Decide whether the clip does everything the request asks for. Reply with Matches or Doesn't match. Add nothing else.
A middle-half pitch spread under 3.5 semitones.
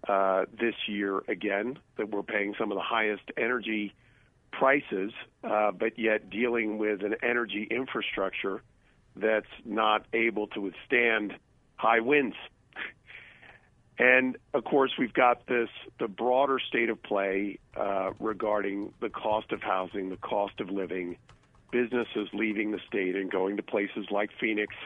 Matches